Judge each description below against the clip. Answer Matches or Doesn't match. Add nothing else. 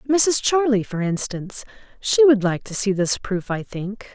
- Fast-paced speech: Doesn't match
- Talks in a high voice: Matches